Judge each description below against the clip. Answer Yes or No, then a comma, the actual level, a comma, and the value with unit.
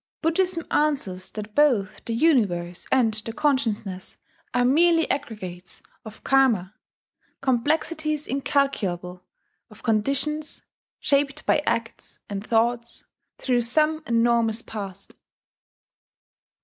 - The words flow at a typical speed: No, slow, 95 wpm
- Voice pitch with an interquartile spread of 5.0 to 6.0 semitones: Yes, wide, 5.5 semitones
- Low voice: No, high, 235 Hz